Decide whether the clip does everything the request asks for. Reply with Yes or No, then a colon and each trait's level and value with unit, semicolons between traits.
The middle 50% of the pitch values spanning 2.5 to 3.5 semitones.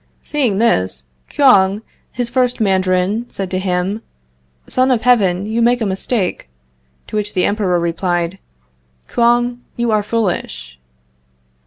No: average, 4.4 semitones